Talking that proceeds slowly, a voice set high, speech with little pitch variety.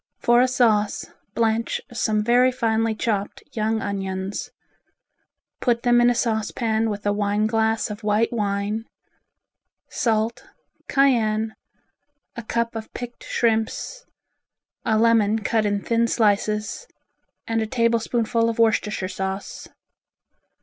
Yes: slow, 120 wpm; high, 220 Hz; narrow, 1.7 semitones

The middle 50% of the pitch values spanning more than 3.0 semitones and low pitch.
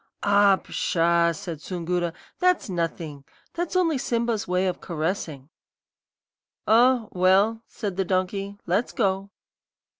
No: average, 4.4 semitones; high, 190 Hz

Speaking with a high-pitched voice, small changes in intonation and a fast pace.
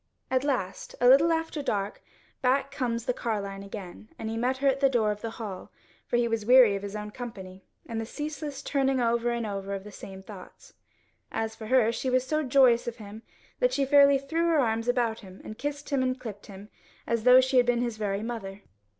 No: high, 235 Hz; average, 4.0 semitones; fast, 220 wpm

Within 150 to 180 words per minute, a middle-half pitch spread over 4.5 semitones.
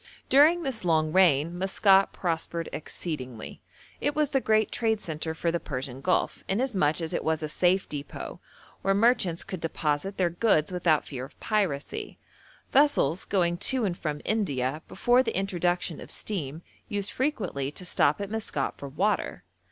Yes: average, 160 wpm; wide, 5.4 semitones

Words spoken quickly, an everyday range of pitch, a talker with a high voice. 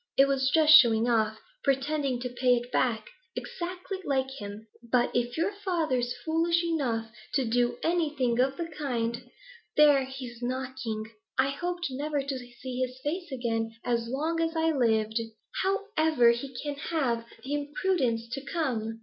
No: average, 160 wpm; average, 4.4 semitones; very high, 260 Hz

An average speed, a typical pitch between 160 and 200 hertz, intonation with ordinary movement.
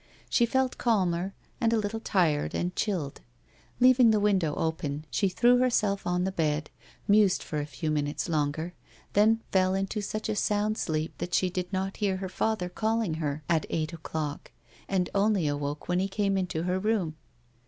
Yes: average, 180 wpm; medium, 185 Hz; average, 4.8 semitones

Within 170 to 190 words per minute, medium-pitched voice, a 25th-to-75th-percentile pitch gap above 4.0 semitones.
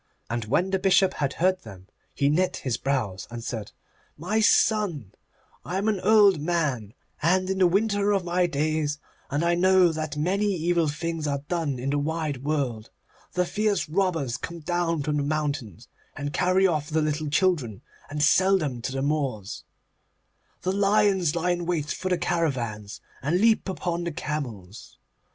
Yes: average, 175 wpm; medium, 160 Hz; average, 4.6 semitones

